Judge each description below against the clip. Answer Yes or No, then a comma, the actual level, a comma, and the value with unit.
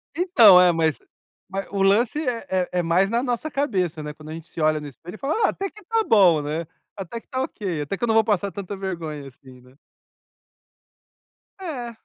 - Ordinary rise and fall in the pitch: No, wide, 6.6 semitones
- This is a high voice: Yes, high, 195 Hz